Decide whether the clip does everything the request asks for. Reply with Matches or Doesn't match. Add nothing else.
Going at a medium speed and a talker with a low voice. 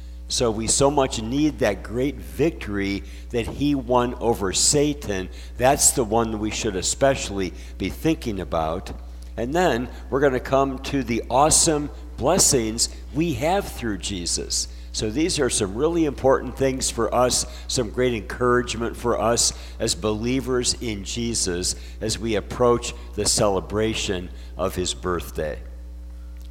Matches